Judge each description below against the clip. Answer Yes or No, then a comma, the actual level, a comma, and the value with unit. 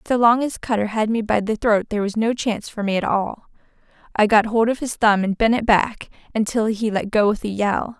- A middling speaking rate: No, fast, 255 wpm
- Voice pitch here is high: Yes, high, 215 Hz